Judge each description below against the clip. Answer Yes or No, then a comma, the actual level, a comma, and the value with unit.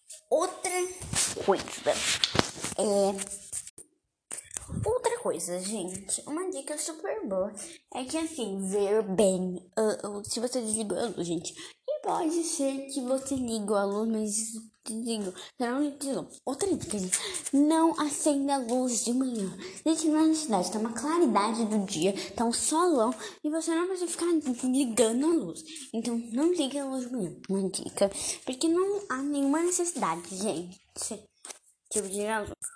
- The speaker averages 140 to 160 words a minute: Yes, average, 145 wpm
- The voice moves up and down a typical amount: No, wide, 7.4 semitones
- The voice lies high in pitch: Yes, very high, 250 Hz